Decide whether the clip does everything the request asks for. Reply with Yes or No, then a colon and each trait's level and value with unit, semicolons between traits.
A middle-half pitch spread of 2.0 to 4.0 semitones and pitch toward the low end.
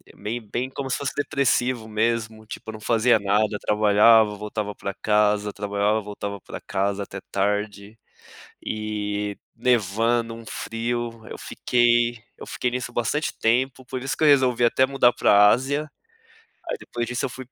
Yes: average, 2.8 semitones; low, 115 Hz